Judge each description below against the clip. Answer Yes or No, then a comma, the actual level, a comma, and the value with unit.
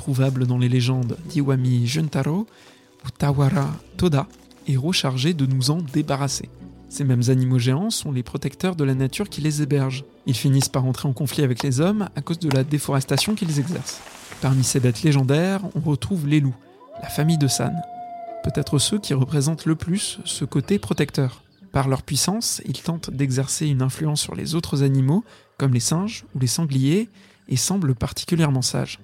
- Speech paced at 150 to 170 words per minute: No, average, 180 wpm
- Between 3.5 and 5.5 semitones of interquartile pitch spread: Yes, average, 3.9 semitones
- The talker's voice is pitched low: No, medium, 145 Hz